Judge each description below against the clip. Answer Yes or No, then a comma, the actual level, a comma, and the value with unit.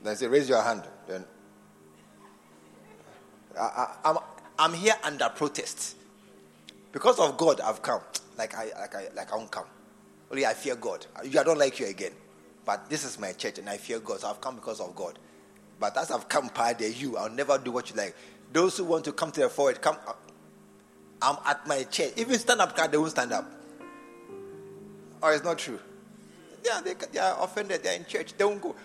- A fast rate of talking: Yes, fast, 210 wpm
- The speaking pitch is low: No, medium, 155 Hz